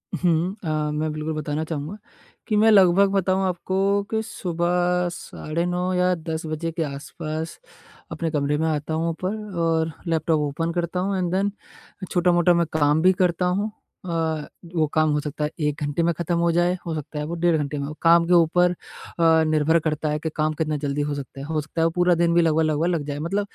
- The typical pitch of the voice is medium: Yes, medium, 165 Hz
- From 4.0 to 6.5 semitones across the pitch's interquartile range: No, narrow, 2.5 semitones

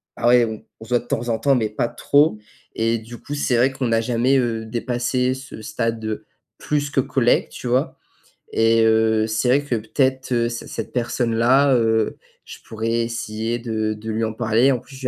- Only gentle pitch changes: Yes, narrow, 2.2 semitones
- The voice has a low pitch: Yes, low, 120 Hz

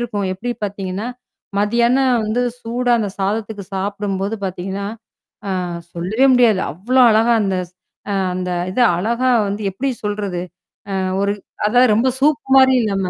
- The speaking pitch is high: Yes, high, 210 Hz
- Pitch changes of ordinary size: Yes, average, 3.7 semitones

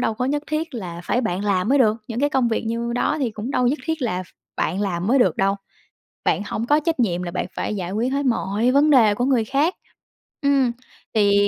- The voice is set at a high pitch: Yes, high, 235 Hz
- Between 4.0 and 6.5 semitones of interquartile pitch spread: Yes, average, 5.2 semitones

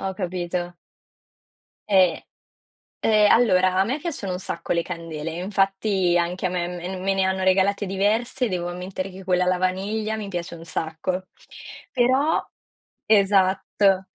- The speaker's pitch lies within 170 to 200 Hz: Yes, high, 190 Hz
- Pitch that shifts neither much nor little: No, narrow, 2.0 semitones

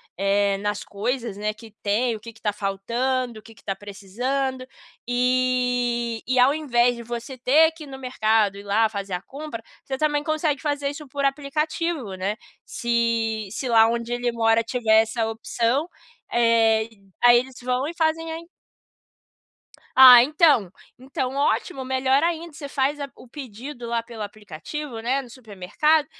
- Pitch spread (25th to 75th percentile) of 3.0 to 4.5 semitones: Yes, average, 4.0 semitones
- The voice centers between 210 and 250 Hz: Yes, high, 245 Hz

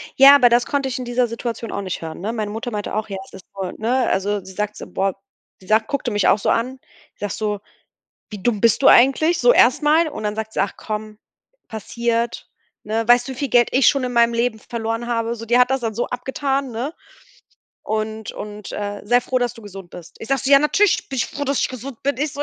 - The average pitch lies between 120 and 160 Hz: No, high, 235 Hz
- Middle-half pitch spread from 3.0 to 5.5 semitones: Yes, average, 3.4 semitones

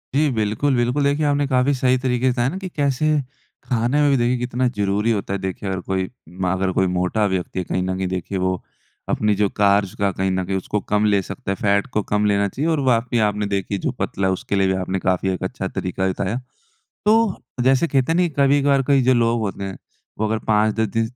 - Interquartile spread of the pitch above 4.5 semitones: Yes, average, 5.2 semitones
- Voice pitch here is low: Yes, low, 105 Hz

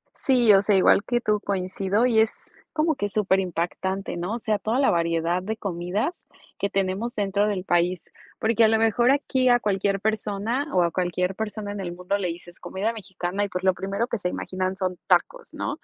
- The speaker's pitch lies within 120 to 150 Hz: No, high, 200 Hz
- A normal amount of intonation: Yes, average, 3.1 semitones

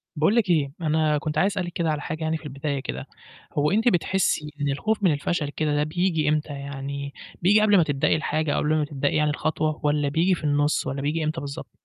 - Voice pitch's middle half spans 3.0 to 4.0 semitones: No, narrow, 2.6 semitones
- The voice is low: No, medium, 155 Hz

